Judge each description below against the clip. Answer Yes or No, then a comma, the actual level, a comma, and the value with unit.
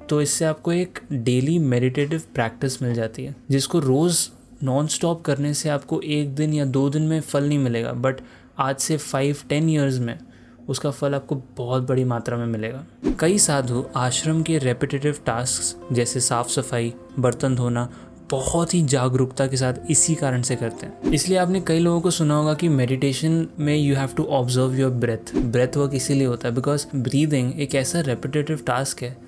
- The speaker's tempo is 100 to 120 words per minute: No, average, 185 wpm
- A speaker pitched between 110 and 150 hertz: Yes, low, 135 Hz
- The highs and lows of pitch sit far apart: No, average, 3.1 semitones